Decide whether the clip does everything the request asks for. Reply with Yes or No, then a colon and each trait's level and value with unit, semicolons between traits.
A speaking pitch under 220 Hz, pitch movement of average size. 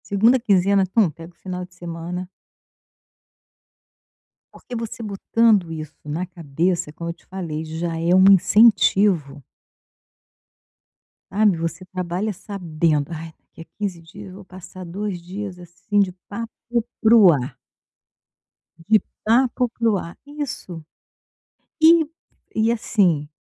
Yes: medium, 185 Hz; average, 4.0 semitones